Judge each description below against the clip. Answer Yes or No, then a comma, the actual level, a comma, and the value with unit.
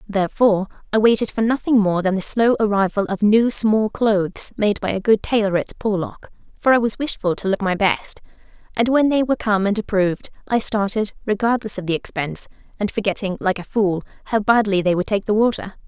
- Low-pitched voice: No, high, 210 Hz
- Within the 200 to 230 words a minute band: Yes, fast, 205 wpm